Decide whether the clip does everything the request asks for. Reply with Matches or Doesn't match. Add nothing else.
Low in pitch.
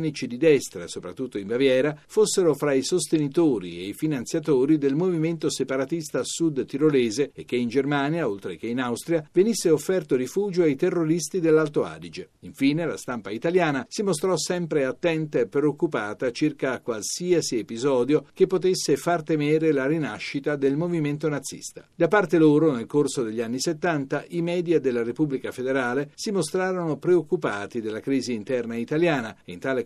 Doesn't match